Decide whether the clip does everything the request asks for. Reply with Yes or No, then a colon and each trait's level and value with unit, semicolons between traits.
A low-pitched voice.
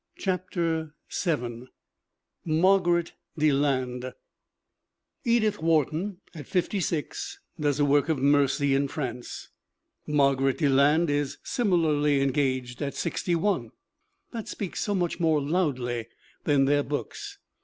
No: medium, 150 Hz